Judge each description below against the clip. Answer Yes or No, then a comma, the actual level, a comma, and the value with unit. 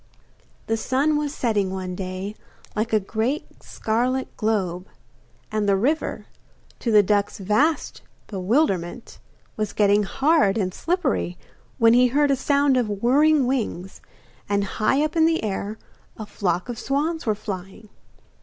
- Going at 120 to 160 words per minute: Yes, average, 145 wpm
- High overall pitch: Yes, high, 220 Hz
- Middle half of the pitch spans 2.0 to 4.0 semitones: No, wide, 5.4 semitones